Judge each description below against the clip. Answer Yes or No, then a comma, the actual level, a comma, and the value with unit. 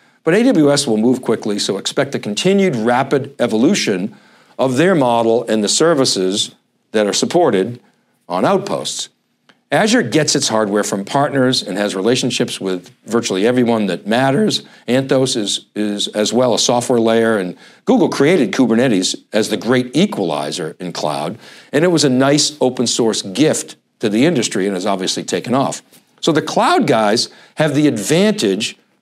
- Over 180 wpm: No, average, 160 wpm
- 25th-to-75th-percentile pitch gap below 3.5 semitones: No, average, 4.3 semitones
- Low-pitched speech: Yes, low, 125 Hz